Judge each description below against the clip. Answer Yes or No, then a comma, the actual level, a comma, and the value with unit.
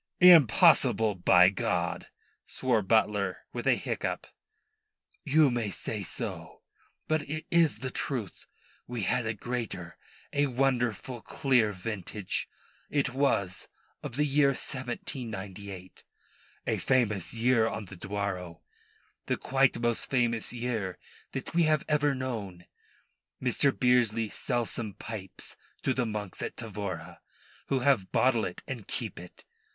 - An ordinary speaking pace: No, slow, 130 wpm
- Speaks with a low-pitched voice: Yes, low, 115 Hz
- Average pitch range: Yes, average, 4.6 semitones